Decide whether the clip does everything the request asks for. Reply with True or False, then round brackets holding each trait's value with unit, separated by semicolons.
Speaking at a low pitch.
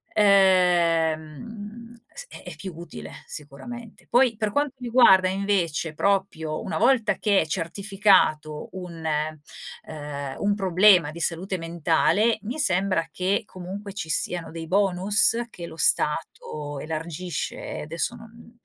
False (185 Hz)